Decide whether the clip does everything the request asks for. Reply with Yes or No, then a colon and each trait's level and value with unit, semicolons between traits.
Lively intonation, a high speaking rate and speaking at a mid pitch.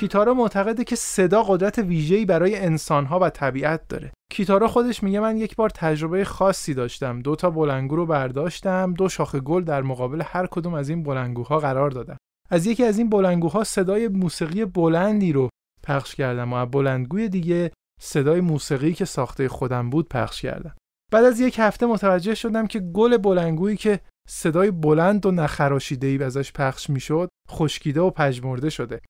Yes: wide, 5.9 semitones; fast, 170 wpm; medium, 170 Hz